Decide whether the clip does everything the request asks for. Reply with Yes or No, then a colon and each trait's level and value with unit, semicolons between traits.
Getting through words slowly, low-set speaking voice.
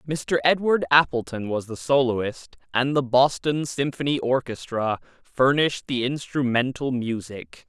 Yes: slow, 115 wpm; low, 130 Hz